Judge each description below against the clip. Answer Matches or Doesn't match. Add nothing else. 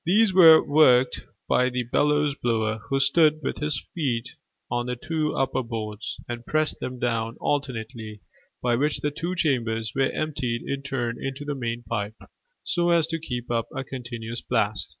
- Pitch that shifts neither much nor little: Matches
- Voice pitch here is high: Doesn't match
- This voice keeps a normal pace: Matches